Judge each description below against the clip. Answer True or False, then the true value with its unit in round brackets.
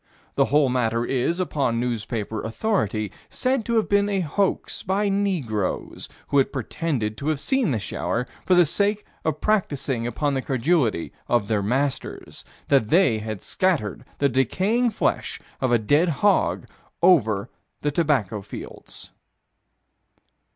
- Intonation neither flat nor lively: False (8.3 semitones)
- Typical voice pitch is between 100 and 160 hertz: True (140 Hz)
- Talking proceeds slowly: False (145 wpm)